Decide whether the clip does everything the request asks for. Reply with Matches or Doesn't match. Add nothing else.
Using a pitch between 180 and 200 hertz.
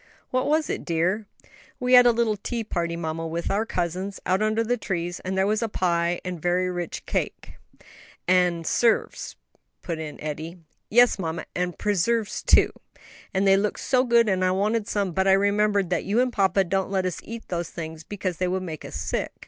Matches